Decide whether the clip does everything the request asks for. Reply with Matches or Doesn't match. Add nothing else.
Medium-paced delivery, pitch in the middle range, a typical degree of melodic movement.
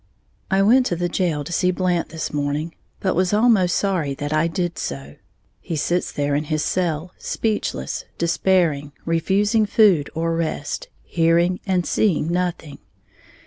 Matches